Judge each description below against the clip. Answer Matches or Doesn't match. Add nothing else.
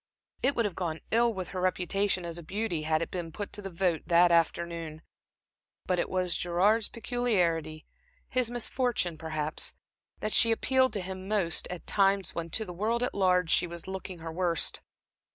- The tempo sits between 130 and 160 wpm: Doesn't match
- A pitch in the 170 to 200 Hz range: Matches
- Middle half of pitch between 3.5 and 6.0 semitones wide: Matches